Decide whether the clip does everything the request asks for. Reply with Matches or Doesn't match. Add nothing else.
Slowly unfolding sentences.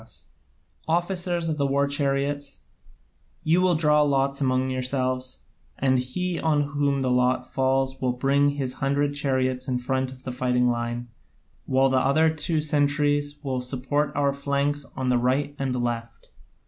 Doesn't match